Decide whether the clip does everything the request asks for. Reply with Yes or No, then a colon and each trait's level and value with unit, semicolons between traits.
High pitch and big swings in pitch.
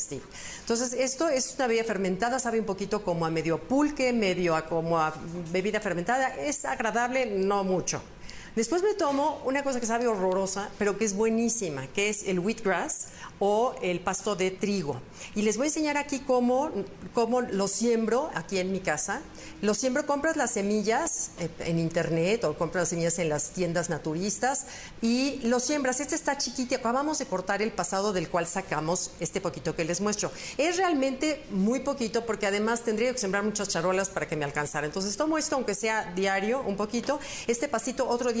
Yes: high, 210 Hz; wide, 5.9 semitones